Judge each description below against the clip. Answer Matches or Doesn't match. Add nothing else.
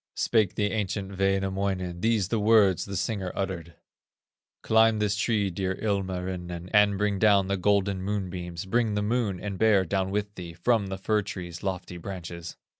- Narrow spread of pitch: Matches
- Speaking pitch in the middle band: Doesn't match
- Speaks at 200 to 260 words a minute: Doesn't match